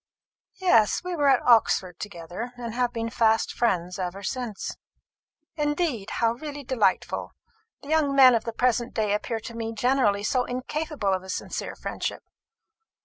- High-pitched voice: Yes, high, 235 Hz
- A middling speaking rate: Yes, average, 155 wpm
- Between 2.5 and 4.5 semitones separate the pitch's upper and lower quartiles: Yes, average, 4.2 semitones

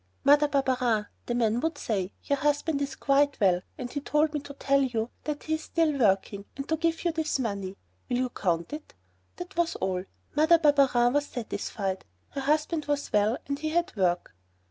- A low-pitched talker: No, very high, 275 Hz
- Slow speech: No, average, 190 wpm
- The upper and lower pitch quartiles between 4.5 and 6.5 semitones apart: Yes, average, 5.2 semitones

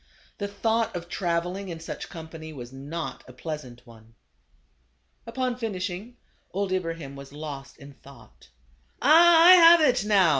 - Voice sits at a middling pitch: Yes, medium, 170 Hz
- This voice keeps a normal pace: Yes, average, 155 wpm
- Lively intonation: Yes, wide, 7.9 semitones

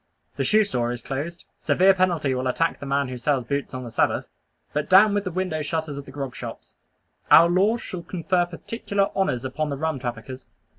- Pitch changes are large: Yes, wide, 5.7 semitones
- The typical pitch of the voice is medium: Yes, medium, 155 Hz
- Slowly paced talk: No, fast, 205 wpm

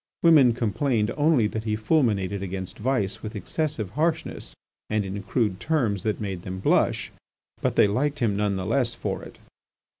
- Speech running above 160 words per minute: Yes, average, 170 wpm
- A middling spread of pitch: Yes, average, 4.9 semitones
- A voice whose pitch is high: No, low, 110 Hz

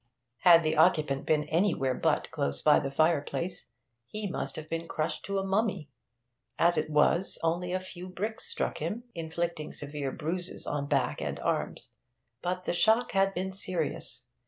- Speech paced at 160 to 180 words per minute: Yes, average, 165 wpm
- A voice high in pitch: No, medium, 170 Hz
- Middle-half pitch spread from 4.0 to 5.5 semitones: No, average, 3.6 semitones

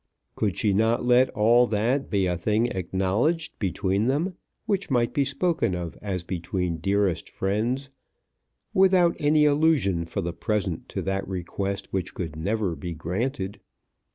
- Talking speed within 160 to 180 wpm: No, average, 150 wpm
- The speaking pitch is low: Yes, low, 105 Hz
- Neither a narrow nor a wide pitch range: No, wide, 6.0 semitones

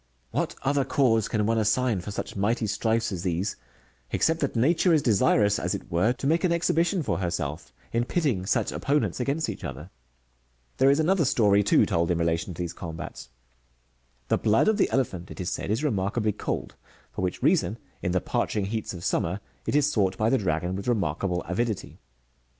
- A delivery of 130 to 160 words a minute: No, average, 200 wpm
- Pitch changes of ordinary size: No, wide, 6.7 semitones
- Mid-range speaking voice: No, low, 105 Hz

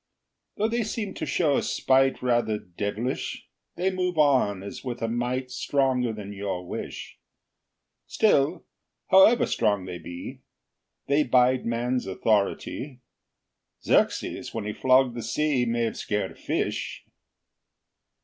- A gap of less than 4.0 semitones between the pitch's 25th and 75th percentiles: No, average, 4.8 semitones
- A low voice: Yes, low, 125 Hz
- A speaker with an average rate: No, slow, 130 wpm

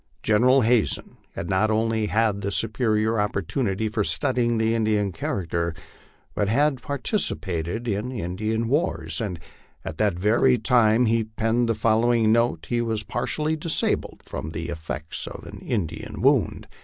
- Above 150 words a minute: No, average, 145 wpm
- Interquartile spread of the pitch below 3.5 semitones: Yes, average, 3.0 semitones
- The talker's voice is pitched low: Yes, low, 110 Hz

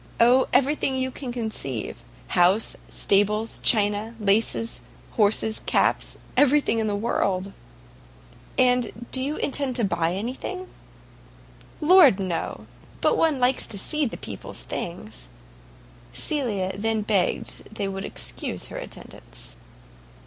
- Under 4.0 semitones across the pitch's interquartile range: No, average, 4.7 semitones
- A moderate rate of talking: No, slow, 125 wpm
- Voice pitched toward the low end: No, high, 220 Hz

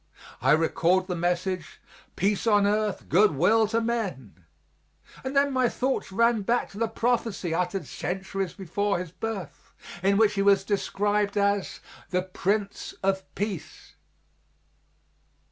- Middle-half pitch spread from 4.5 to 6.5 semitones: No, average, 3.0 semitones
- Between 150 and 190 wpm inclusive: No, slow, 135 wpm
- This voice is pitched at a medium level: No, high, 200 Hz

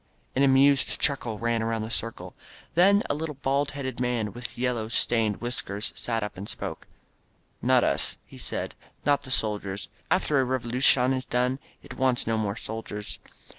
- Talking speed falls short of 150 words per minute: No, average, 170 wpm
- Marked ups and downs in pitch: No, average, 3.2 semitones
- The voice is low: Yes, low, 125 Hz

